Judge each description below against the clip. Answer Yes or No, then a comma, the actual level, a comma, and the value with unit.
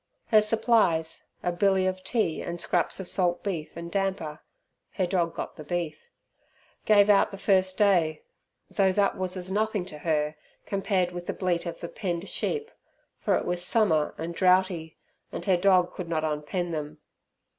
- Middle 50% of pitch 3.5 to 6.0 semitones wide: No, average, 2.7 semitones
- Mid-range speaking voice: Yes, medium, 180 Hz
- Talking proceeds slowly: No, average, 175 wpm